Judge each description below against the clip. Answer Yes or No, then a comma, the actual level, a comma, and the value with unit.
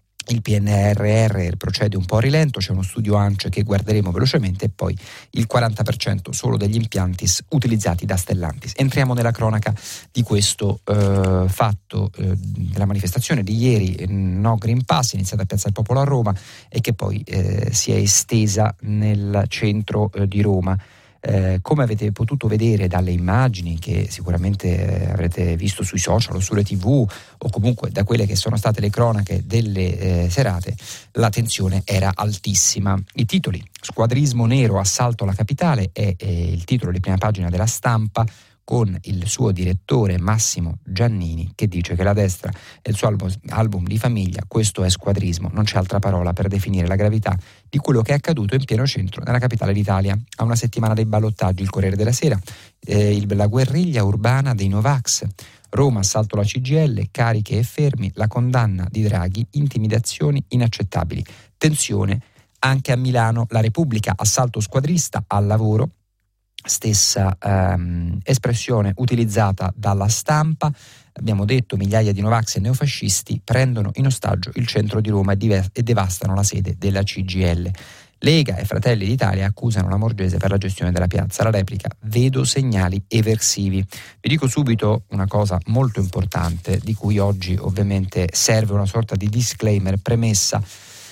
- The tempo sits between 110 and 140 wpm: No, average, 165 wpm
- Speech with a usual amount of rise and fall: Yes, average, 3.1 semitones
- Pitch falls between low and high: No, low, 105 Hz